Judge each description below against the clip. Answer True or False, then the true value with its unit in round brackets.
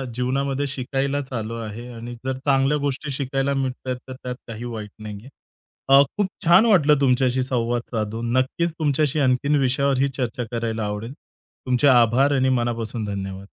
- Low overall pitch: True (130 Hz)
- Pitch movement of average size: True (3.0 semitones)